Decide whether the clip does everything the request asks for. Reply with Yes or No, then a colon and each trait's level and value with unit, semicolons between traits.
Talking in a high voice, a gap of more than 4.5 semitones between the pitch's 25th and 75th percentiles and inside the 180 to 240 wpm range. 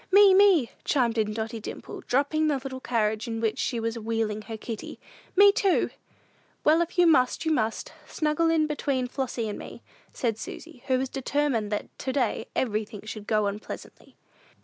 Yes: very high, 250 Hz; wide, 5.5 semitones; average, 185 wpm